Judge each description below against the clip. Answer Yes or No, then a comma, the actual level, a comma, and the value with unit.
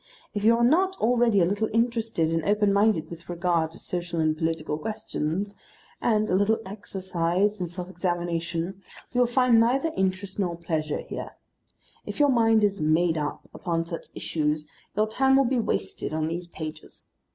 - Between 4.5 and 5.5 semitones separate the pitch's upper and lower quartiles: Yes, average, 4.9 semitones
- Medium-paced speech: Yes, average, 175 wpm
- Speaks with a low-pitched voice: No, high, 190 Hz